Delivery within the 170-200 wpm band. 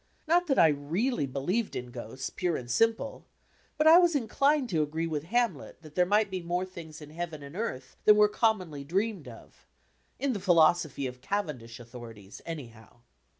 Yes: average, 180 wpm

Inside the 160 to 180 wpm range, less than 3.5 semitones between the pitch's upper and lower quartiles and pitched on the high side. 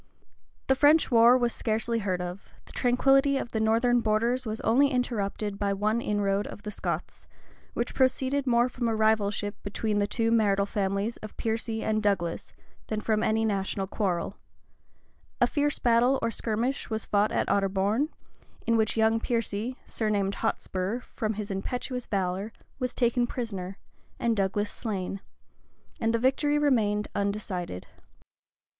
No: average, 150 wpm; average, 3.1 semitones; high, 220 Hz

